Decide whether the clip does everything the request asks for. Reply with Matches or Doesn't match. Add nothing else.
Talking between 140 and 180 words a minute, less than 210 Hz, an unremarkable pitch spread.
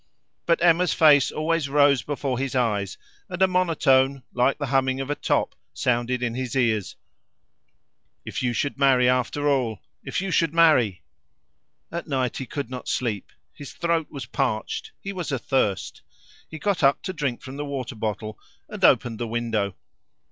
Matches